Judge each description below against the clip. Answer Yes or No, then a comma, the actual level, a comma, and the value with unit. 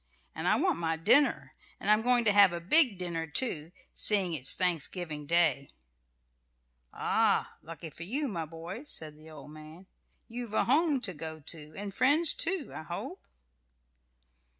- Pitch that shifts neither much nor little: No, wide, 6.6 semitones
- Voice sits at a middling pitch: Yes, medium, 175 Hz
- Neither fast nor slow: Yes, average, 160 wpm